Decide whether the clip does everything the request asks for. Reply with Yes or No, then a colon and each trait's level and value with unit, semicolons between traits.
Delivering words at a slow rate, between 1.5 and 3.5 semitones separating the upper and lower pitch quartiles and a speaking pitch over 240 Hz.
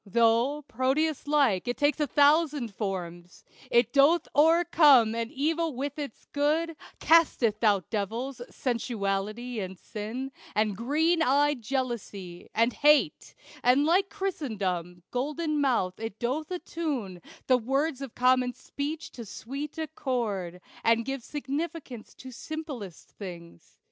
No: slow, 125 wpm; average, 5.3 semitones; very high, 255 Hz